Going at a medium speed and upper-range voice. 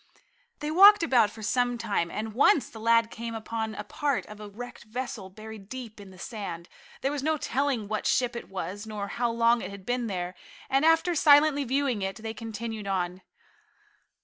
Yes: average, 195 wpm; high, 230 Hz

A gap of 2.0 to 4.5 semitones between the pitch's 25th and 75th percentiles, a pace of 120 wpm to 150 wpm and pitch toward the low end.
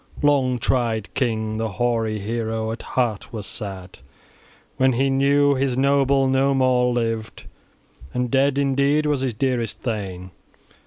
Yes: average, 3.5 semitones; average, 140 wpm; low, 125 Hz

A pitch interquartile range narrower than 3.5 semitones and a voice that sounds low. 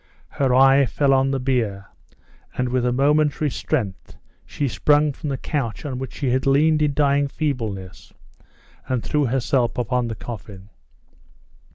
Yes: average, 2.8 semitones; low, 130 Hz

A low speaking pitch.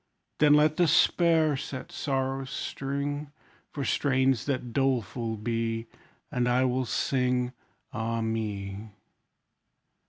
Yes: low, 130 Hz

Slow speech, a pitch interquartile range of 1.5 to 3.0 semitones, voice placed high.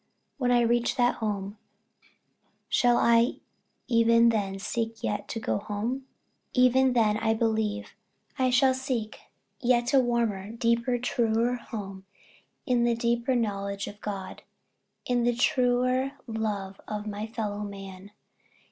Yes: slow, 130 wpm; average, 2.7 semitones; high, 230 Hz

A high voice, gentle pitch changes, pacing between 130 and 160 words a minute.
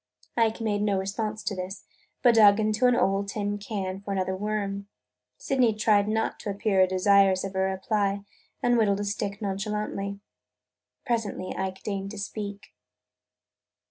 Yes: high, 200 Hz; narrow, 1.5 semitones; average, 150 wpm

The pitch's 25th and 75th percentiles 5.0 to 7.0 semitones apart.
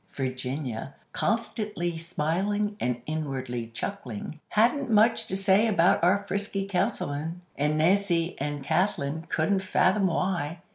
Yes: wide, 5.4 semitones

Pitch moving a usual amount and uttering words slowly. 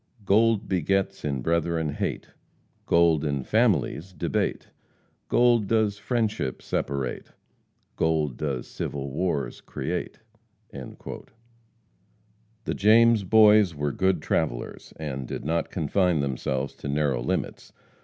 No: wide, 6.8 semitones; slow, 105 wpm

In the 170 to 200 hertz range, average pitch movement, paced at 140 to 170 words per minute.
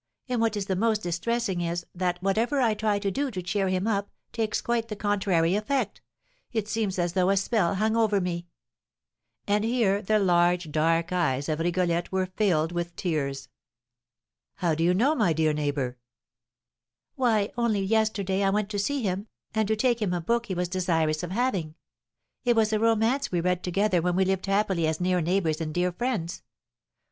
No: high, 190 Hz; average, 3.9 semitones; average, 190 wpm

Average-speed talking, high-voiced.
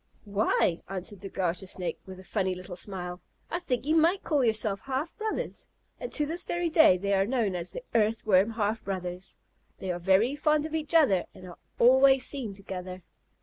Yes: average, 190 wpm; high, 205 Hz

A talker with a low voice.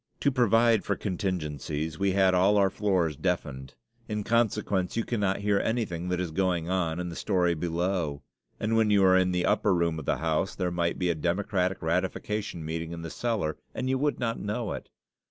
Yes: very low, 95 Hz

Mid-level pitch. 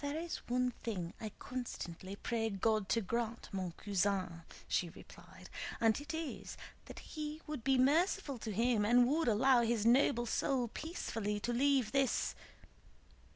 No: high, 235 Hz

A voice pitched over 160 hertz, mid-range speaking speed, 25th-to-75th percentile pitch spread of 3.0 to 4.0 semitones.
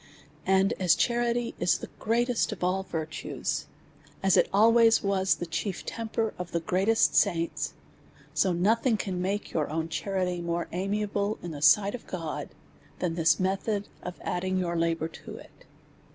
Yes: high, 190 Hz; average, 170 wpm; average, 3.5 semitones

